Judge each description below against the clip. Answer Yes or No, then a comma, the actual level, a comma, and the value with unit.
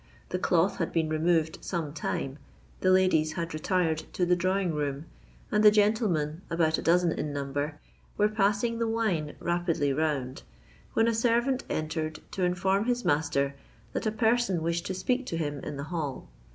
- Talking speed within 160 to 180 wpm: Yes, average, 165 wpm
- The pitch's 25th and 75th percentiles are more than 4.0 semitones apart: Yes, average, 4.7 semitones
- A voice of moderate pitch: Yes, medium, 170 Hz